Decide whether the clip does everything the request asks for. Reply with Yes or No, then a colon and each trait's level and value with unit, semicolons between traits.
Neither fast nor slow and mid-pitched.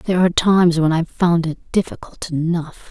Yes: average, 185 wpm; medium, 170 Hz